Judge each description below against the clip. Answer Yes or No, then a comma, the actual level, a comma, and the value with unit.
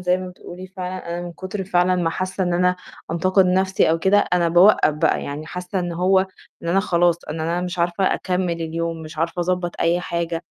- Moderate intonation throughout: No, narrow, 1.6 semitones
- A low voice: No, medium, 175 Hz